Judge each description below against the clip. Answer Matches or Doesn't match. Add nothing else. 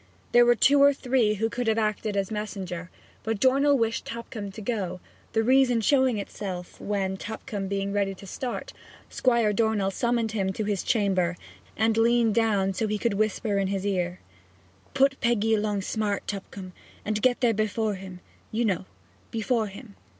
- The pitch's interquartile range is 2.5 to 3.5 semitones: Matches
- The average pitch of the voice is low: Doesn't match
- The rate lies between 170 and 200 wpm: Matches